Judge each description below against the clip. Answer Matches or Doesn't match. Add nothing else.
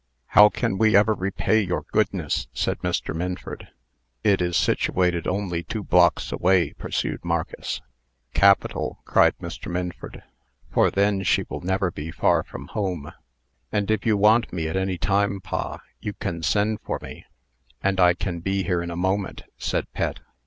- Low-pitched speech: Matches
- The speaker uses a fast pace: Doesn't match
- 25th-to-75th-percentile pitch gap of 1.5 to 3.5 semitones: Matches